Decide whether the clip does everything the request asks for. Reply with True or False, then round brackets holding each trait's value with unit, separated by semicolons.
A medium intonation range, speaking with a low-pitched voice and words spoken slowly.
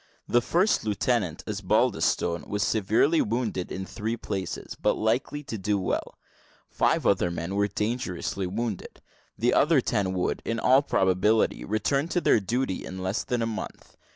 False (4.2 semitones; 110 Hz; 155 wpm)